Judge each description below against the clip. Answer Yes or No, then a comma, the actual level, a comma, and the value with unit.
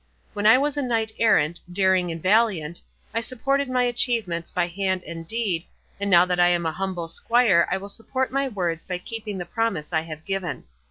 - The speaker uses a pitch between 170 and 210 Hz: Yes, high, 190 Hz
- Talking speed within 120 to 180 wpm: No, fast, 205 wpm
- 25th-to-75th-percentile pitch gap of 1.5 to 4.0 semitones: No, average, 4.9 semitones